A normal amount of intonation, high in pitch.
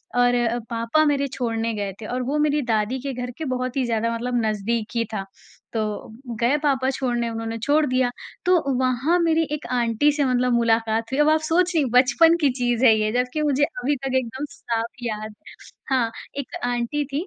Yes: average, 3.7 semitones; very high, 250 Hz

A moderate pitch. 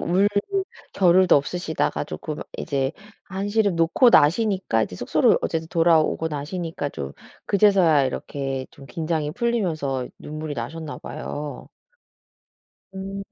Yes: medium, 160 Hz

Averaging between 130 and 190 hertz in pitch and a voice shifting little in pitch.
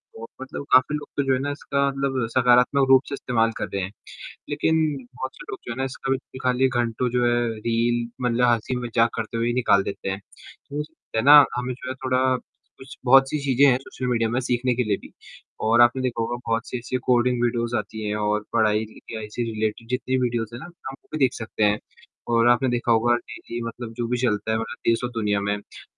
No: low, 120 Hz; narrow, 2.2 semitones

